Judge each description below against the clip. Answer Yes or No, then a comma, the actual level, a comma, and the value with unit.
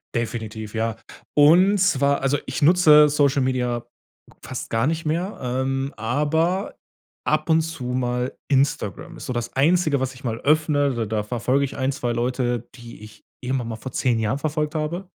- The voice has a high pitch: No, low, 130 Hz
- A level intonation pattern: No, average, 4.0 semitones